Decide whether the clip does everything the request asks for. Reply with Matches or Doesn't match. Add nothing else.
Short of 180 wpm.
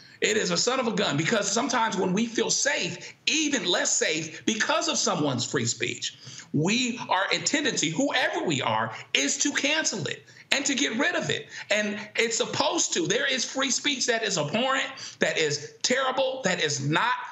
Doesn't match